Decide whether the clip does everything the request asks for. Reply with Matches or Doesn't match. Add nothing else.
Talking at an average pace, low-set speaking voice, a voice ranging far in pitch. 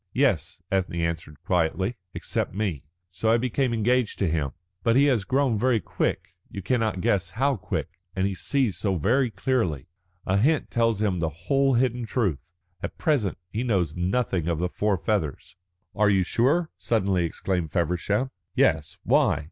Matches